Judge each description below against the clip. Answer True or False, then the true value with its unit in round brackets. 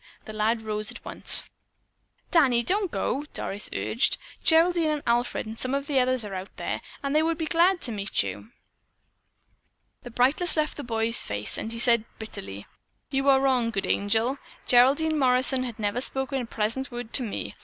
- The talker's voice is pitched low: False (245 Hz)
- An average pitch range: True (4.2 semitones)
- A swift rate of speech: False (185 wpm)